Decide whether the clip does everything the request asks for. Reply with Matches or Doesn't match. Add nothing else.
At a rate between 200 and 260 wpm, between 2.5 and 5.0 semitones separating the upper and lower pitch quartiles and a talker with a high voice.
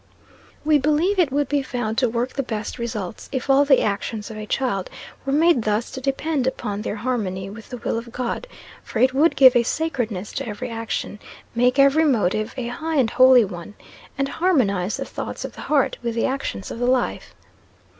Matches